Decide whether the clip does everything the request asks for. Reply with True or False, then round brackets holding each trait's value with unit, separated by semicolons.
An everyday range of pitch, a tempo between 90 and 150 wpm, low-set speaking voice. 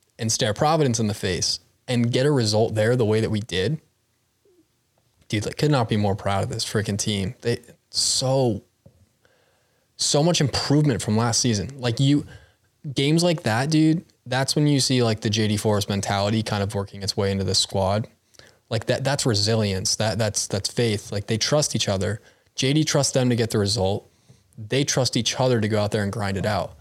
False (4.4 semitones; 200 wpm; 115 Hz)